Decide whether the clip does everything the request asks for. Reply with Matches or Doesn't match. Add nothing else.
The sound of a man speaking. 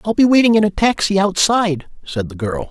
Matches